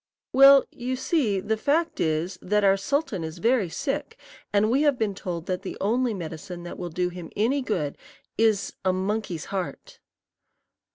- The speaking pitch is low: No, high, 205 Hz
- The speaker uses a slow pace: No, average, 170 wpm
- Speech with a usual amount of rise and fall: No, wide, 6.1 semitones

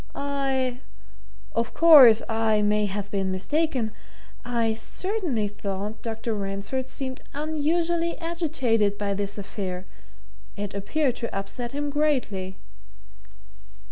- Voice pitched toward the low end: No, high, 230 Hz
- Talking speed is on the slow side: Yes, slow, 110 wpm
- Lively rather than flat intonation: Yes, wide, 5.8 semitones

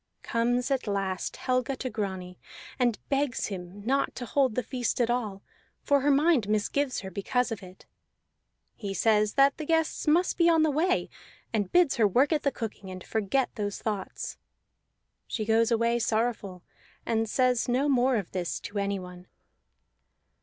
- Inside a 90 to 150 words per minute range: No, average, 165 wpm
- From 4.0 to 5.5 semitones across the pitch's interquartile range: Yes, average, 4.9 semitones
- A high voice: Yes, high, 235 Hz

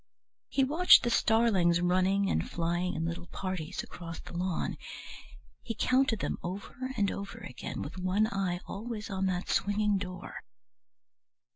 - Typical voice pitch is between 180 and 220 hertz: Yes, high, 190 Hz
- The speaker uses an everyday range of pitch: Yes, average, 3.3 semitones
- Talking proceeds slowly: No, average, 145 wpm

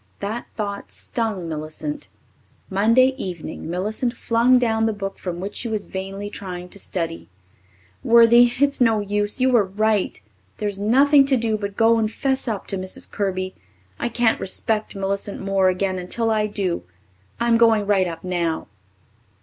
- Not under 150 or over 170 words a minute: Yes, average, 160 wpm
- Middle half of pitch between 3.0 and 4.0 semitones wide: Yes, average, 3.4 semitones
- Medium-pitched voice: No, high, 205 Hz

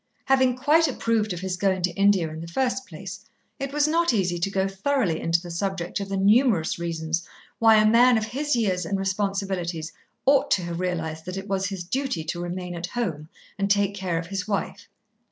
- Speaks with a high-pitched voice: Yes, high, 195 Hz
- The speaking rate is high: Yes, fast, 210 wpm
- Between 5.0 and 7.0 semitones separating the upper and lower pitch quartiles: No, average, 4.4 semitones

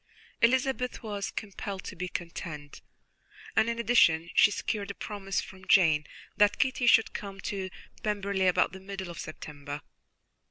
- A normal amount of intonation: Yes, average, 3.4 semitones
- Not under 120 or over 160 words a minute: Yes, average, 150 wpm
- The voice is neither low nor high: No, high, 195 Hz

